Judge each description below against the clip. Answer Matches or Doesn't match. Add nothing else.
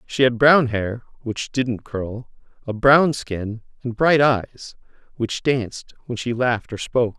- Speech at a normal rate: Matches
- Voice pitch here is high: Doesn't match